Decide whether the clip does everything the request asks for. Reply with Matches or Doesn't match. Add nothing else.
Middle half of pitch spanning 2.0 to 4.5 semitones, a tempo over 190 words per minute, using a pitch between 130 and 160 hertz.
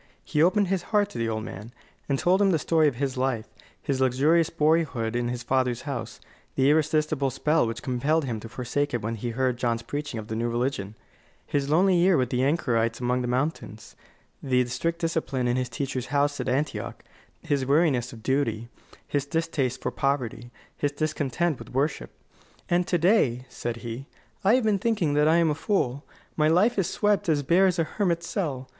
Doesn't match